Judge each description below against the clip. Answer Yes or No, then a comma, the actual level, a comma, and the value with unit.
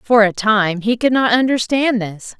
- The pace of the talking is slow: No, average, 200 wpm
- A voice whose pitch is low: No, high, 225 Hz